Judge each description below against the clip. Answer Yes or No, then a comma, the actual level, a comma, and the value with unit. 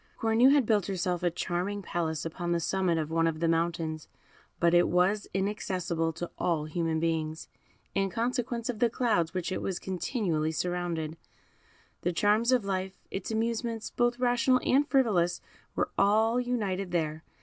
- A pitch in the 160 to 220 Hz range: Yes, medium, 185 Hz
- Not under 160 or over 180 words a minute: Yes, average, 165 wpm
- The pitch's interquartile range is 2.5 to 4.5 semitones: No, average, 5.1 semitones